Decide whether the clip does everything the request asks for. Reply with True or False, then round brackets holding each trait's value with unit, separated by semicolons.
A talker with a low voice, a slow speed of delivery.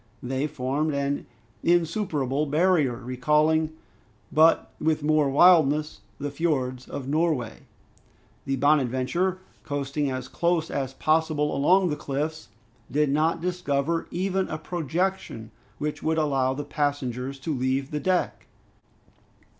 False (150 Hz; 120 wpm)